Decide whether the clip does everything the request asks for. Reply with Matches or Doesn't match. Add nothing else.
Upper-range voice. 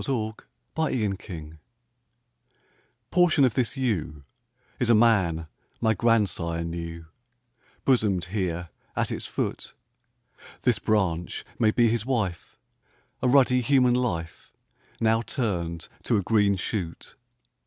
Doesn't match